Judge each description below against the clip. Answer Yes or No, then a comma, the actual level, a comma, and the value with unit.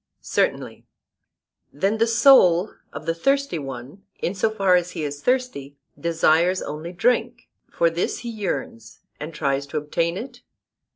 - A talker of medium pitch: Yes, medium, 175 Hz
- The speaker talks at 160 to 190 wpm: No, average, 150 wpm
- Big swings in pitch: Yes, wide, 6.7 semitones